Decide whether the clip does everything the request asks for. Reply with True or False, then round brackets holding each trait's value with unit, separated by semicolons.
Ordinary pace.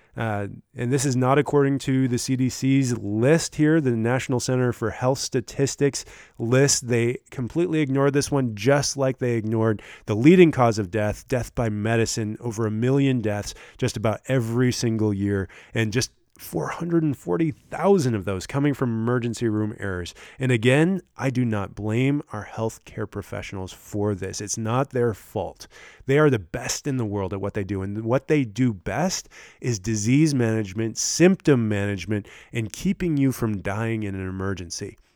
True (165 wpm)